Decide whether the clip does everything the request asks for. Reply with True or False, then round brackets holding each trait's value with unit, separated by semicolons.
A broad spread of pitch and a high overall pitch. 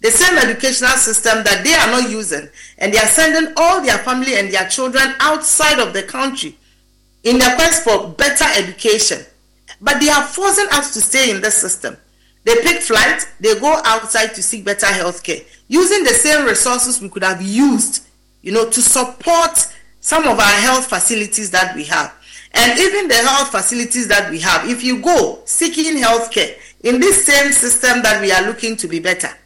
True (6.2 semitones; 250 Hz)